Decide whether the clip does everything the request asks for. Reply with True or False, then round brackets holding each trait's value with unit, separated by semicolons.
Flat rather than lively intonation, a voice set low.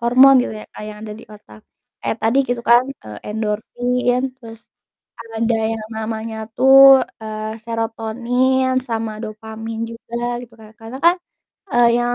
False (1.9 semitones; 225 Hz)